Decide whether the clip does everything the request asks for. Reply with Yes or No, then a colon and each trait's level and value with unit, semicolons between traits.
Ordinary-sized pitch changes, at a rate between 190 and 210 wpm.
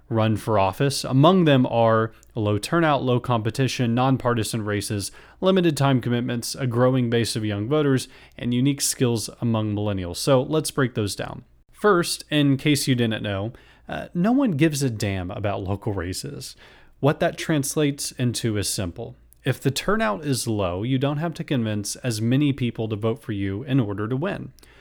No: average, 4.5 semitones; average, 175 wpm